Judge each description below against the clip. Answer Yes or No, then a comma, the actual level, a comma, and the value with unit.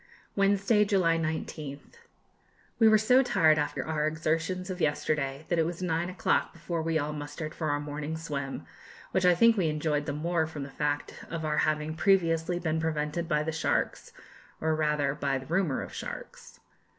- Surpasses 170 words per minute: Yes, average, 180 wpm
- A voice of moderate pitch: Yes, medium, 160 Hz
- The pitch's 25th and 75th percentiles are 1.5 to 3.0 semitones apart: Yes, narrow, 2.5 semitones